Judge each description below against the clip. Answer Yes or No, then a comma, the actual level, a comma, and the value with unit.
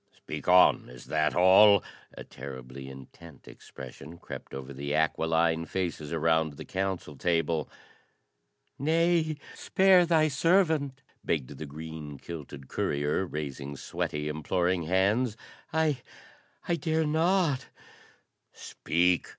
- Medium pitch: No, very low, 85 Hz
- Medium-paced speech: No, slow, 115 wpm